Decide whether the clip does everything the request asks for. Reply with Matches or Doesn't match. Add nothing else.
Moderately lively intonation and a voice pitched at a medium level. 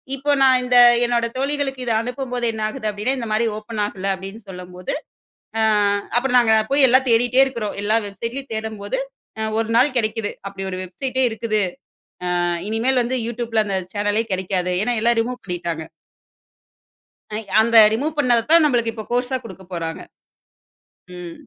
Doesn't match